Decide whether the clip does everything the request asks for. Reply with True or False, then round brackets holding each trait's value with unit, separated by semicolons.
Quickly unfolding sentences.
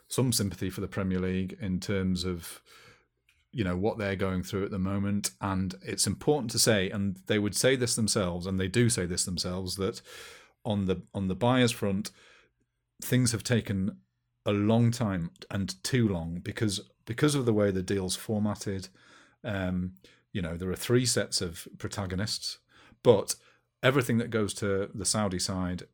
False (175 wpm)